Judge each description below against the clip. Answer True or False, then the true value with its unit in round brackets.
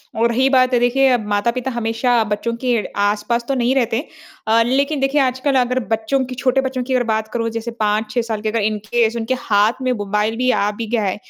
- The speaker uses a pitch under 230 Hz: False (235 Hz)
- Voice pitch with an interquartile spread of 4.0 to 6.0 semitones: False (2.7 semitones)